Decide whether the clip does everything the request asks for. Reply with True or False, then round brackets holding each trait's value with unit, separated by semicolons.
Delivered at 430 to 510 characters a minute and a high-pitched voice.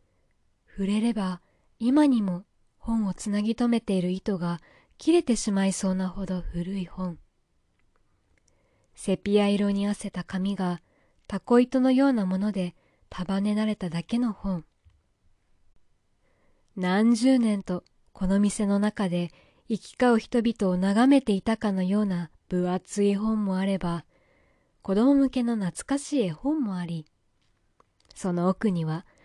False (240 characters per minute; 195 Hz)